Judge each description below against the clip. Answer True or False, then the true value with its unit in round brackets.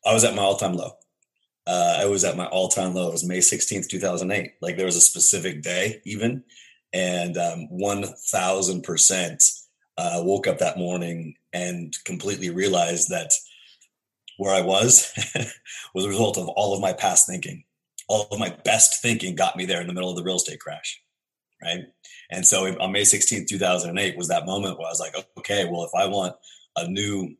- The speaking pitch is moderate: False (95 Hz)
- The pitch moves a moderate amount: False (2.2 semitones)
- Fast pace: False (195 wpm)